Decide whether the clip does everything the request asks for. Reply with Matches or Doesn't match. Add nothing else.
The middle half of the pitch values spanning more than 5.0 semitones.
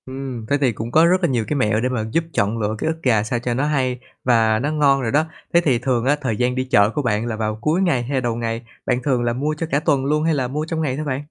Doesn't match